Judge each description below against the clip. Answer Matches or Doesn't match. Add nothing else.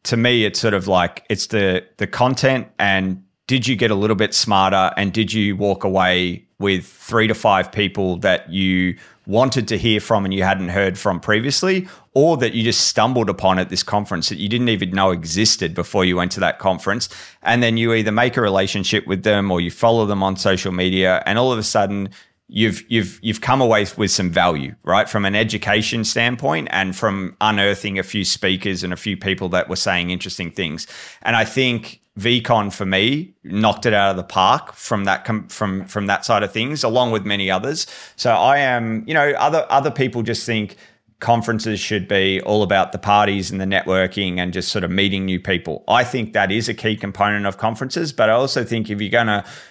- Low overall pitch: Matches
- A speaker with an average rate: Doesn't match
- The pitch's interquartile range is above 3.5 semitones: Doesn't match